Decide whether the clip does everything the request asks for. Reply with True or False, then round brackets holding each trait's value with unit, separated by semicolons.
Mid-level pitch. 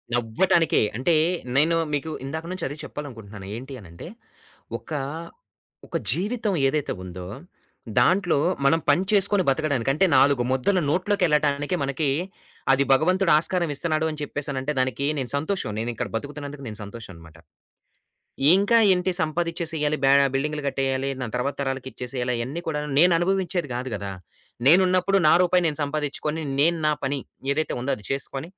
True (145 Hz)